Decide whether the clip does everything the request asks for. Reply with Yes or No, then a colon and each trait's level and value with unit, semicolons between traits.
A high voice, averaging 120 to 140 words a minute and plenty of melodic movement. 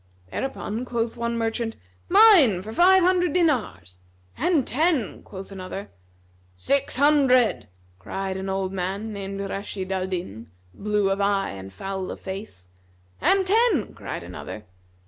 Yes: high, 210 Hz; slow, 135 wpm; wide, 6.3 semitones